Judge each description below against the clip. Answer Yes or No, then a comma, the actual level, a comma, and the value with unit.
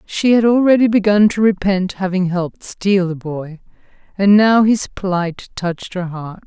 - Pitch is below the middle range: No, high, 195 Hz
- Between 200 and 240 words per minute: No, average, 165 wpm